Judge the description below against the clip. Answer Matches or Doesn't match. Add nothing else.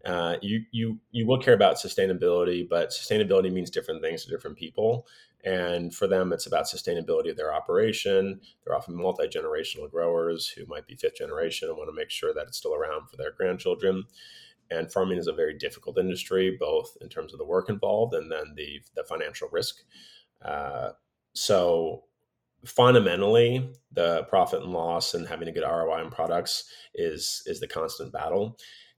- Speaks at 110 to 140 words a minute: Doesn't match